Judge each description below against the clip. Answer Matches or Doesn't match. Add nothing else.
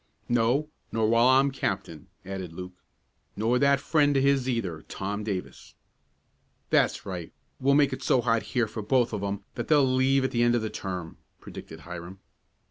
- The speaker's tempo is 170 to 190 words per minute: Matches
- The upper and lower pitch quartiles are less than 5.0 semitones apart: Doesn't match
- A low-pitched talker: Matches